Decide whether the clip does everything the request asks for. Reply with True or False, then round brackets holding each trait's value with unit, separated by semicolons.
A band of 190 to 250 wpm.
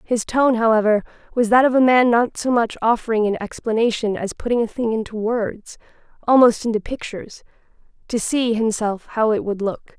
False (170 wpm)